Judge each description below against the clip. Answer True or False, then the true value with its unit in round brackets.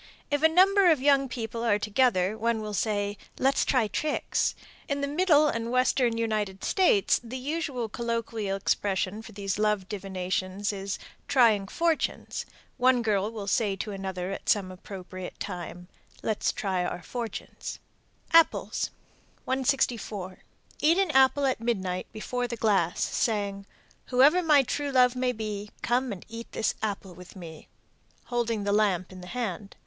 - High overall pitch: True (220 Hz)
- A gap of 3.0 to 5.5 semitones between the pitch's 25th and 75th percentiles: True (4.5 semitones)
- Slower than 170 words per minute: True (155 wpm)